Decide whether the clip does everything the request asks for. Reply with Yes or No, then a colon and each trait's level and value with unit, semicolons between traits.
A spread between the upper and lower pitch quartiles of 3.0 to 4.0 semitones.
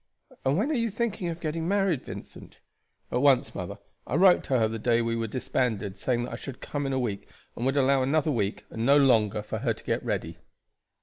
No: wide, 5.4 semitones